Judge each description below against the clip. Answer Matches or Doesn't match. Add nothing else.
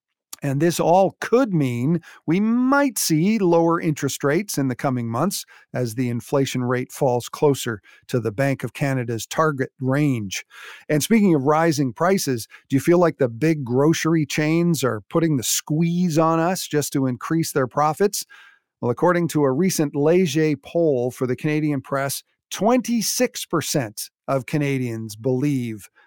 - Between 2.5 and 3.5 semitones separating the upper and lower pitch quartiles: Doesn't match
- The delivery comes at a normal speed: Matches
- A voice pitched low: Doesn't match